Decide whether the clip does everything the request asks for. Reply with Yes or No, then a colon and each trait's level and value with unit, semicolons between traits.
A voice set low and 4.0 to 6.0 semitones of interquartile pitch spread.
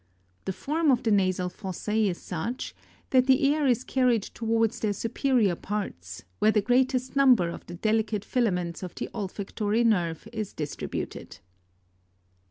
No: high, 215 Hz; average, 4.9 semitones